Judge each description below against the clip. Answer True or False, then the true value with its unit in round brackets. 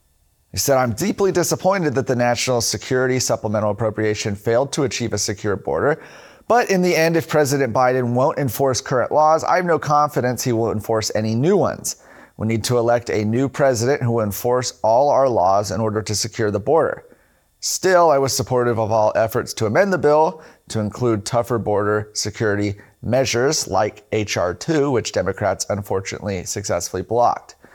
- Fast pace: False (175 wpm)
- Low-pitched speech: True (120 Hz)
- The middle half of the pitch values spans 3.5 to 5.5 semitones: True (4.2 semitones)